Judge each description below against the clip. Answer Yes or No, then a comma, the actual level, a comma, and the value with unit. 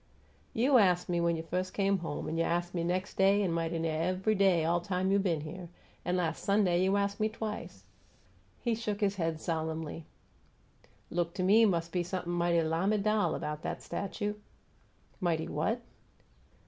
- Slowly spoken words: No, average, 175 wpm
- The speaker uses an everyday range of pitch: Yes, average, 3.1 semitones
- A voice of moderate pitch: Yes, medium, 180 Hz